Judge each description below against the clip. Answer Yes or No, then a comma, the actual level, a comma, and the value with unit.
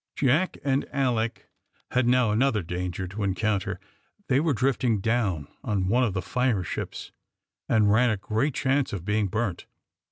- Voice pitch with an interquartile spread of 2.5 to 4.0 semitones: No, average, 4.6 semitones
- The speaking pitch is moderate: No, low, 110 Hz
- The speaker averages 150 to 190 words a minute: Yes, average, 160 wpm